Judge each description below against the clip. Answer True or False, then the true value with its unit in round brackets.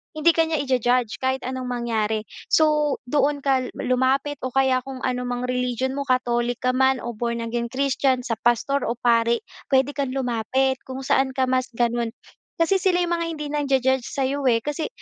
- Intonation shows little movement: True (2.3 semitones)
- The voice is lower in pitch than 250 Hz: False (260 Hz)